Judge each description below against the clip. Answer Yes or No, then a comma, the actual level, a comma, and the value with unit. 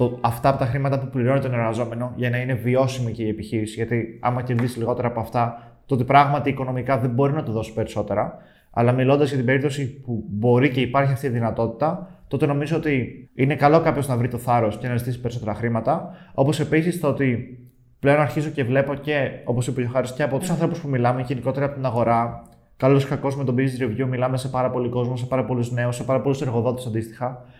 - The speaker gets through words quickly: Yes, fast, 220 wpm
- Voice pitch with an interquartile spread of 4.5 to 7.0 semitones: No, narrow, 2.4 semitones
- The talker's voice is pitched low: Yes, low, 130 Hz